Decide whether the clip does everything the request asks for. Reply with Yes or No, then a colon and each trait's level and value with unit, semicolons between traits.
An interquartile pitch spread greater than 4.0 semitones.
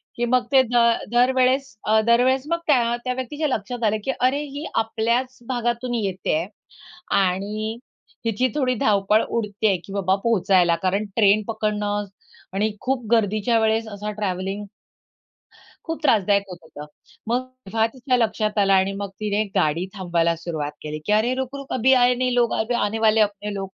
No: average, 3.7 semitones